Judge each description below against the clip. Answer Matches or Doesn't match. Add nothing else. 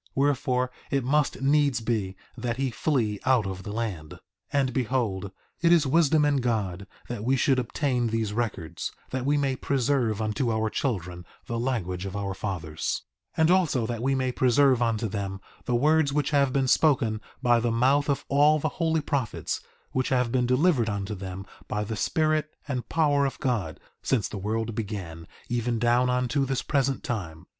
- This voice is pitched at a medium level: Doesn't match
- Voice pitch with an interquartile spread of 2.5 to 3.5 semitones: Doesn't match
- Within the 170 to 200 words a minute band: Matches